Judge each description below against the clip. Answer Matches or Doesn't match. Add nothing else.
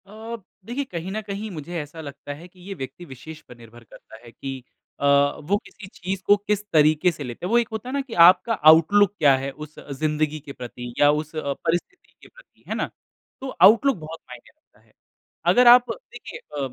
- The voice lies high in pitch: Doesn't match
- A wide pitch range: Matches